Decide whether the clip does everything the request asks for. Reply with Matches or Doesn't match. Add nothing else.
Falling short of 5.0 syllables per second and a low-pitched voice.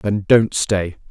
Matches